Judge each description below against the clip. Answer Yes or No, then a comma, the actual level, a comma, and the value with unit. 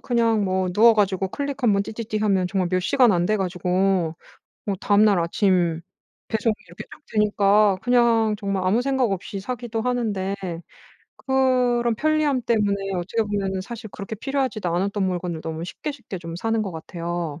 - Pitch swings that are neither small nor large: Yes, average, 4.0 semitones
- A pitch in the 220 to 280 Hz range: No, high, 205 Hz